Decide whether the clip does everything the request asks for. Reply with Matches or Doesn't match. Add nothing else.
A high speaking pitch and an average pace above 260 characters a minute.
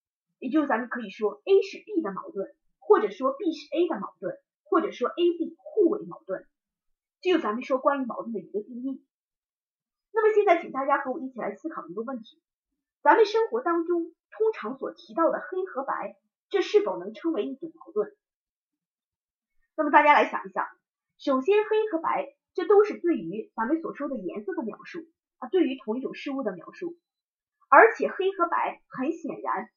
Matches